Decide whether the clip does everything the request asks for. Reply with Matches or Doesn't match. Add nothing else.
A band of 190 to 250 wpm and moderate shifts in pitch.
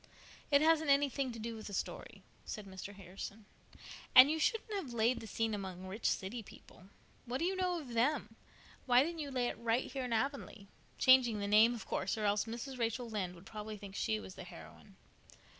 Matches